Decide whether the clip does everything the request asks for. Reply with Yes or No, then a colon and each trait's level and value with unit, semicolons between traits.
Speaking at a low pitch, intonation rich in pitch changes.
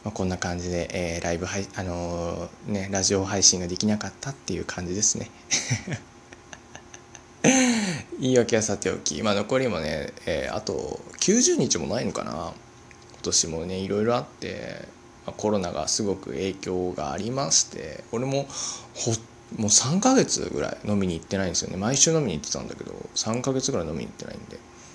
No: low, 100 Hz; average, 4.5 semitones